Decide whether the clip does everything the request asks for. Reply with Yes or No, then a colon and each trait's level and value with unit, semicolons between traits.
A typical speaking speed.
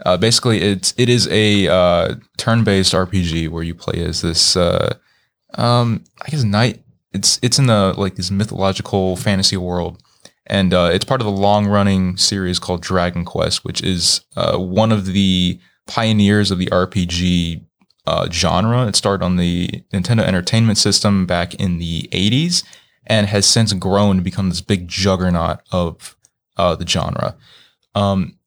Yes: average, 160 wpm